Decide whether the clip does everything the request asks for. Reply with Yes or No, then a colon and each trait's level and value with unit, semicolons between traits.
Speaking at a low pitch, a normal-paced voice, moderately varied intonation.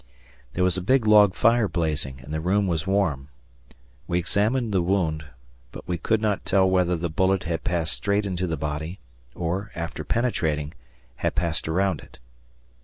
Yes: very low, 90 Hz; average, 175 wpm; average, 3.9 semitones